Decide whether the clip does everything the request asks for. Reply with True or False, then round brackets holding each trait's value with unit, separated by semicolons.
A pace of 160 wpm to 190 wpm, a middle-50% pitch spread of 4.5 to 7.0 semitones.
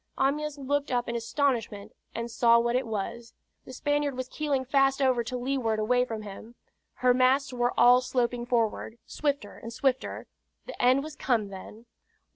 False (170 wpm; 2.7 semitones)